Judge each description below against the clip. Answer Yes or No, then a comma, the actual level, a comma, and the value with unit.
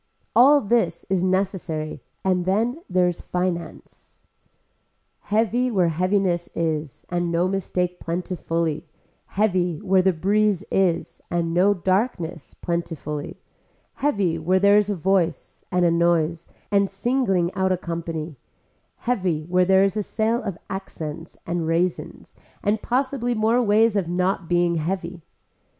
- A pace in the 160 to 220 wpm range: No, slow, 135 wpm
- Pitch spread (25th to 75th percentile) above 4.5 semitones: No, average, 3.0 semitones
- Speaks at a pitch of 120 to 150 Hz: No, medium, 185 Hz